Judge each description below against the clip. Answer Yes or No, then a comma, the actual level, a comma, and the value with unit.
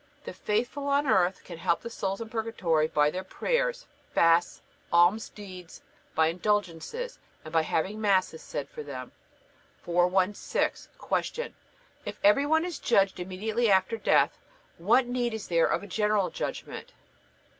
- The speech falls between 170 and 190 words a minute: No, average, 145 wpm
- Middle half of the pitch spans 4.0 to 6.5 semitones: Yes, average, 5.0 semitones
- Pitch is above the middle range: Yes, high, 195 Hz